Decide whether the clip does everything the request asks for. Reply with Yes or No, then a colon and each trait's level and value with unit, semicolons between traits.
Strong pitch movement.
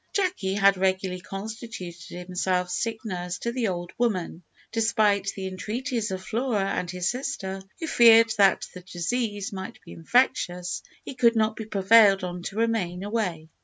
No: average, 3.9 semitones